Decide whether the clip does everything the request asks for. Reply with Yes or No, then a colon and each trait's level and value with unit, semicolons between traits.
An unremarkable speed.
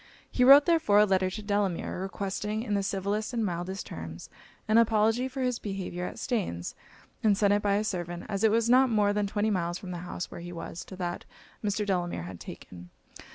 No: fast, 210 wpm